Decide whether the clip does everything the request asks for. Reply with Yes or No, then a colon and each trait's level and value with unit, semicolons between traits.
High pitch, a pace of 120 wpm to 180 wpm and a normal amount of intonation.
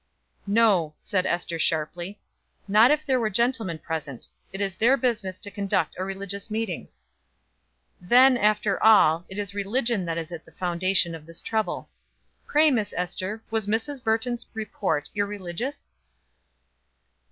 Yes: high, 200 Hz; average, 140 wpm; average, 4.3 semitones